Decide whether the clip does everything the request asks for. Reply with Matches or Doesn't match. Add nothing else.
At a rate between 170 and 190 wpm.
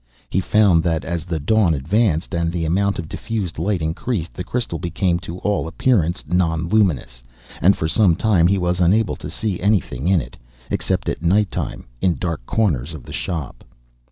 Matches